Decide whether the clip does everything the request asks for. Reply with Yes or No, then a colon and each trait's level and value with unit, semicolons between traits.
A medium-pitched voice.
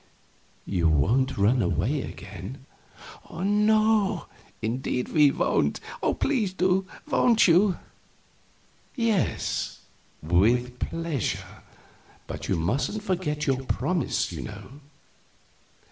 Yes: medium, 150 Hz